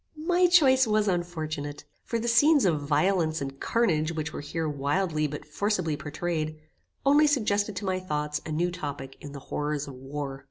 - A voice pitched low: No, medium, 160 Hz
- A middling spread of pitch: No, wide, 5.8 semitones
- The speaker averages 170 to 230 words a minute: Yes, average, 175 wpm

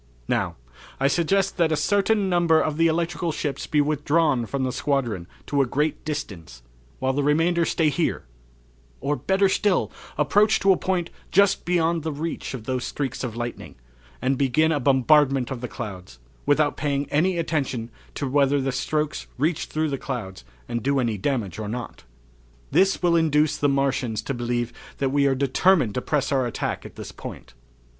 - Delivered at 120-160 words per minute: No, average, 180 wpm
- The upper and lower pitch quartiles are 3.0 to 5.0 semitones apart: Yes, average, 4.2 semitones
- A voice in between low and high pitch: Yes, medium, 145 Hz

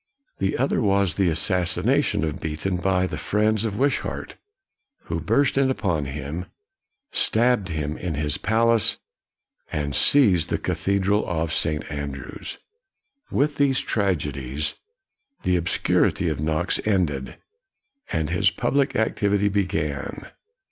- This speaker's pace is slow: Yes, slow, 120 wpm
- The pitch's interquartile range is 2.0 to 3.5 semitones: No, wide, 5.6 semitones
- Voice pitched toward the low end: Yes, very low, 95 Hz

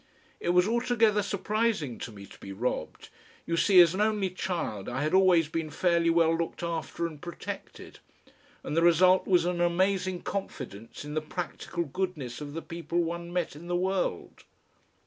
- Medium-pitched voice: Yes, medium, 170 Hz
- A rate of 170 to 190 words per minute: Yes, average, 175 wpm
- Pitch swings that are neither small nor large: Yes, average, 3.2 semitones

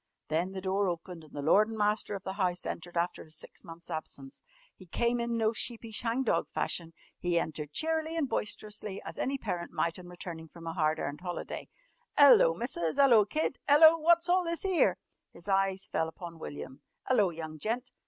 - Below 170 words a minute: No, average, 195 wpm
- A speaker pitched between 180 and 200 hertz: Yes, high, 190 Hz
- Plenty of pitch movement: Yes, wide, 6.1 semitones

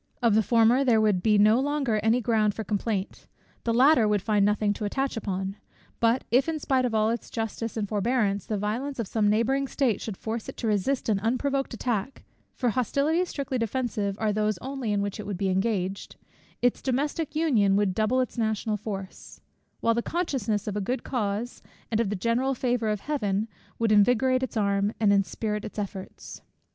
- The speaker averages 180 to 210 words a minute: Yes, average, 195 wpm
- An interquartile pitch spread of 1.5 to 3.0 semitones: No, average, 3.5 semitones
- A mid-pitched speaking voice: No, high, 220 Hz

